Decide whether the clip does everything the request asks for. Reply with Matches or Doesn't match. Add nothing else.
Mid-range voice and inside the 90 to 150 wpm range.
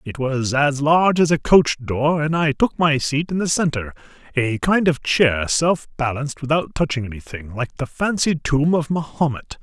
Doesn't match